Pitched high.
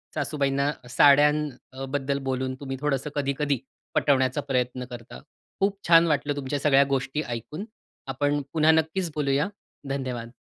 No: medium, 140 Hz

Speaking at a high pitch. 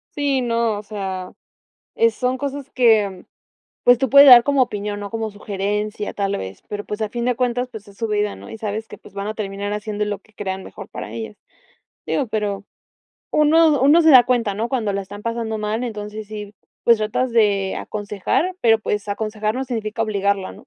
Yes: high, 215 Hz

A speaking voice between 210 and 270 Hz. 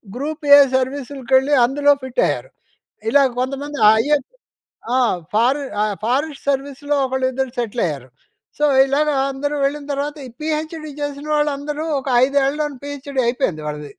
No: very high, 280 Hz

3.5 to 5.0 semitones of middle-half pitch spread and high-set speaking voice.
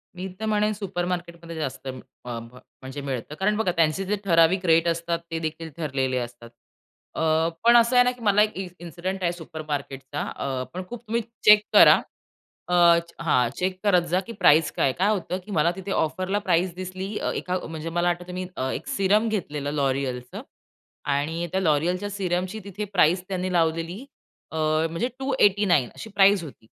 No: average, 4.0 semitones; medium, 175 Hz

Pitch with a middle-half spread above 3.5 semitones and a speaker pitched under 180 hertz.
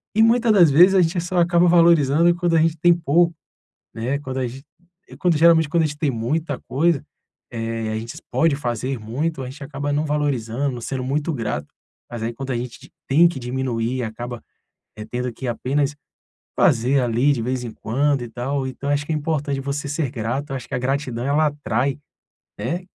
Yes: average, 4.4 semitones; medium, 140 Hz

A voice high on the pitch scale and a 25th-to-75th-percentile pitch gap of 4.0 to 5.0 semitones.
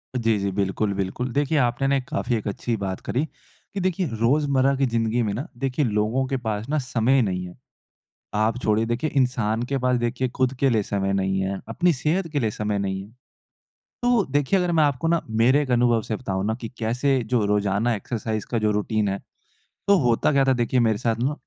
No: low, 120 Hz; average, 4.4 semitones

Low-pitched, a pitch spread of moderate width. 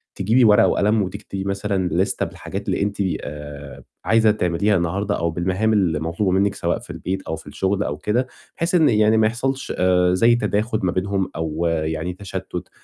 Yes: very low, 95 Hz; average, 3.6 semitones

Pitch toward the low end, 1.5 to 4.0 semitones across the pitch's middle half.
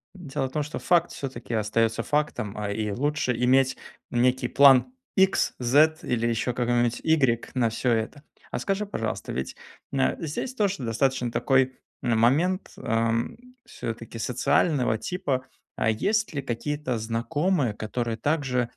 No: low, 125 Hz; average, 4.4 semitones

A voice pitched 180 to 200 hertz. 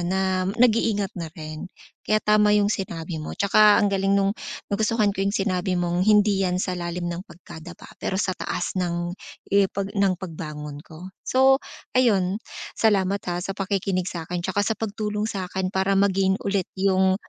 Yes: high, 190 Hz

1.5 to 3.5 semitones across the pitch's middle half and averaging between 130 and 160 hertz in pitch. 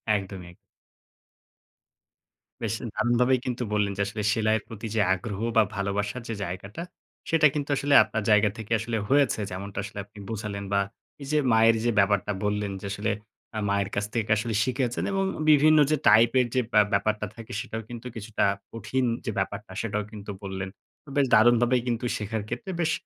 No: average, 3.0 semitones; low, 110 Hz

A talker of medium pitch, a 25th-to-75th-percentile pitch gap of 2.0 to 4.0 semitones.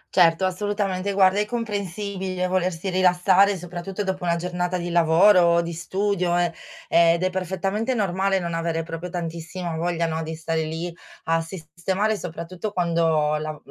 Yes: medium, 180 Hz; narrow, 2.3 semitones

